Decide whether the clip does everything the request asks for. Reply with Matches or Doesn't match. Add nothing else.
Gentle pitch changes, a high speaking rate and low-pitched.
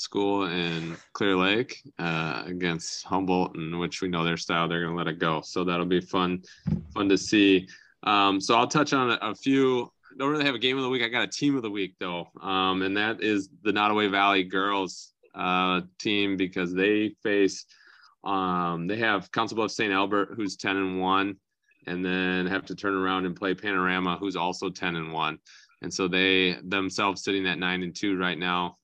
Matches